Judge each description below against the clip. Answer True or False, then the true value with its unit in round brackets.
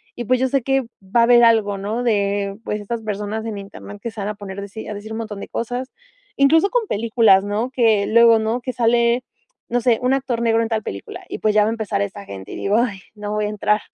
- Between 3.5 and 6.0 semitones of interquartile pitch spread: False (2.7 semitones)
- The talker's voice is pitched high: True (220 Hz)